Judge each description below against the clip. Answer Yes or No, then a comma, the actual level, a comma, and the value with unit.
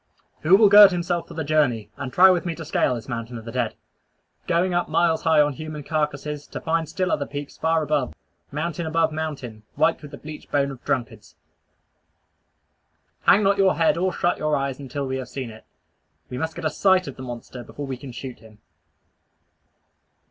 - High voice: No, medium, 150 Hz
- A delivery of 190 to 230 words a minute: Yes, average, 200 wpm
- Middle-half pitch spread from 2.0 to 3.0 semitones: No, average, 4.0 semitones